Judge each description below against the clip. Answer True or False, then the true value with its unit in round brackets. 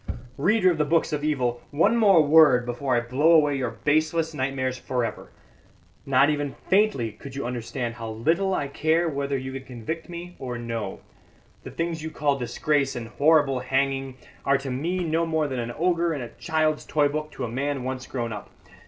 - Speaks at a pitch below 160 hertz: True (140 Hz)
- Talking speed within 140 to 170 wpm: False (195 wpm)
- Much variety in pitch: False (3.9 semitones)